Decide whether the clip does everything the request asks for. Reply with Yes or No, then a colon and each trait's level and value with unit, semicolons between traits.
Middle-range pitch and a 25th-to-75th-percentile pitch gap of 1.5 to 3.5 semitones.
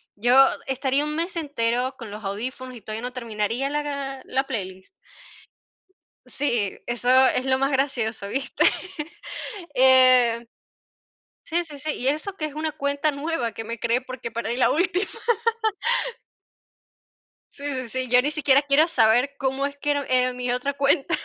No: very high, 260 Hz; average, 3.0 semitones